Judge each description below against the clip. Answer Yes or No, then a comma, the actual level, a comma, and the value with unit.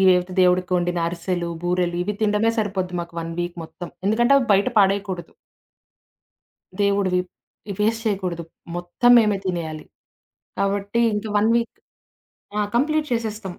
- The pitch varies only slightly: No, average, 3.2 semitones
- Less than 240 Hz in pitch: Yes, high, 195 Hz